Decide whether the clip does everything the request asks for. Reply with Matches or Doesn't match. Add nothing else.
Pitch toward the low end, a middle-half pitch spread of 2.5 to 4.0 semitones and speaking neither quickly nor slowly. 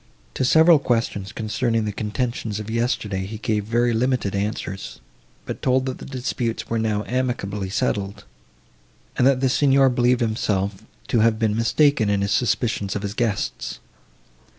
Matches